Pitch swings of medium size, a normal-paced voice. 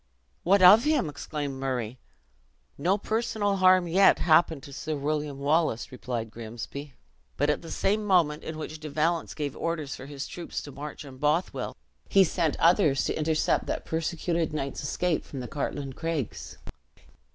Yes: average, 3.8 semitones; average, 165 wpm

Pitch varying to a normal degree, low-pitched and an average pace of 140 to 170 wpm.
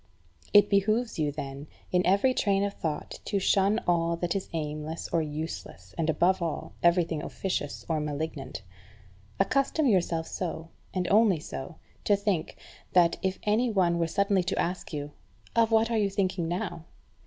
No: average, 3.7 semitones; medium, 175 Hz; average, 165 wpm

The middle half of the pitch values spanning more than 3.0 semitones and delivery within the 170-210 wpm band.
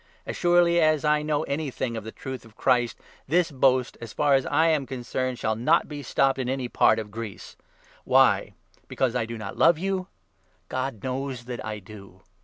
Yes: average, 4.4 semitones; fast, 205 wpm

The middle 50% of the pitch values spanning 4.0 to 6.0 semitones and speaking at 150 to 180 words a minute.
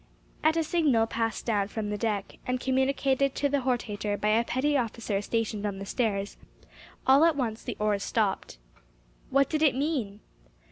Yes: average, 4.7 semitones; average, 175 wpm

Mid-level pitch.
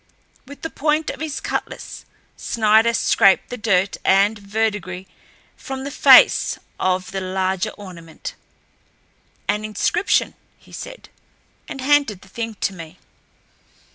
No: high, 210 Hz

